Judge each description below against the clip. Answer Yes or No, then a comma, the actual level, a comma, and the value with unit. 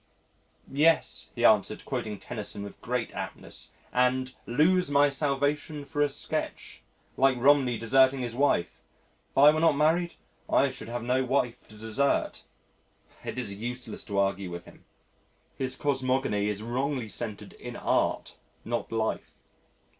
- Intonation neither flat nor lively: Yes, average, 3.9 semitones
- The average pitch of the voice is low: Yes, low, 130 Hz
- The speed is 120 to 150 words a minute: Yes, average, 145 wpm